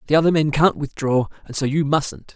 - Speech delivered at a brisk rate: Yes, fast, 230 wpm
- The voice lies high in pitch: No, medium, 150 Hz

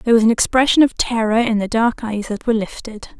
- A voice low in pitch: No, high, 225 Hz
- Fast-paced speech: Yes, fast, 245 wpm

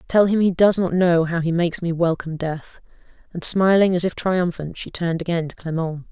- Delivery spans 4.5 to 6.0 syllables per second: Yes, 5.6 syllables/s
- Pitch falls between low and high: Yes, medium, 170 Hz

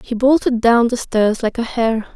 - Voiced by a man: No, female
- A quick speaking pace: Yes, fast, 225 wpm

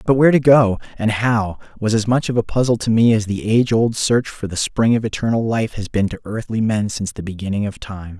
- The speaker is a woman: No, male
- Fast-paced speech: Yes, fast, 255 wpm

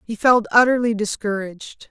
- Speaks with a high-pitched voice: Yes, high, 220 Hz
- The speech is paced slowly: Yes, slow, 125 wpm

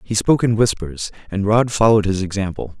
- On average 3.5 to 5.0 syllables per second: No, 6.0 syllables/s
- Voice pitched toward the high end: No, low, 105 Hz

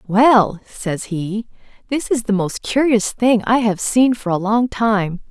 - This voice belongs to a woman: Yes, female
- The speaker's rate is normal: Yes, average, 180 wpm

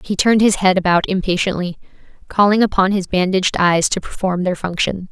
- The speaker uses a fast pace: No, average, 175 wpm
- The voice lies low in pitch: No, high, 190 Hz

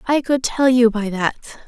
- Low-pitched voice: No, high, 240 Hz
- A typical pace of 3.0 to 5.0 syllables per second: Yes, 4.9 syllables/s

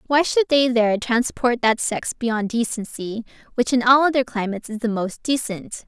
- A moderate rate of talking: Yes, average, 185 wpm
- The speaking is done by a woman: Yes, female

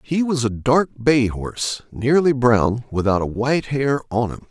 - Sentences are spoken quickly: No, average, 185 wpm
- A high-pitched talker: No, low, 125 Hz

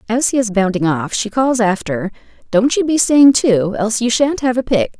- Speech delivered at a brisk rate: Yes, fast, 215 wpm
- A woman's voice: Yes, female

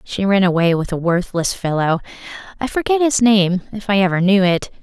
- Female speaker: Yes, female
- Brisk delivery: No, average, 185 wpm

